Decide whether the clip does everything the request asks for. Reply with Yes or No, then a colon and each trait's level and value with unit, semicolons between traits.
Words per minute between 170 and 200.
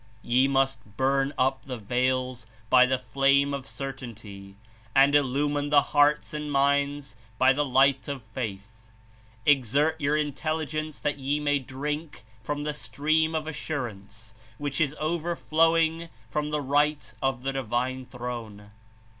No: average, 140 wpm